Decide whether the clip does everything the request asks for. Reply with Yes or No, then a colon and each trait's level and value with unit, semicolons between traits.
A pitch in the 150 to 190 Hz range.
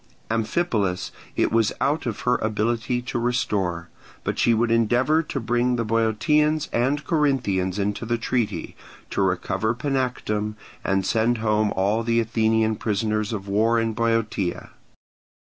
No: low, 115 Hz